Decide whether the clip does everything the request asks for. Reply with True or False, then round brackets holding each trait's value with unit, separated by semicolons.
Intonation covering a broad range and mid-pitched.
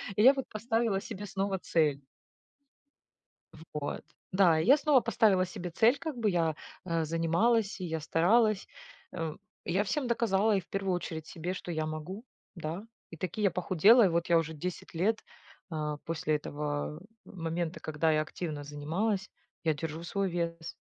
False (4.4 semitones; 175 Hz)